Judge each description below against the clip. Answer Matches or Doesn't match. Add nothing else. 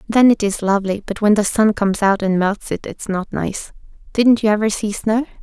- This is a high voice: Matches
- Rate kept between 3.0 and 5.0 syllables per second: Doesn't match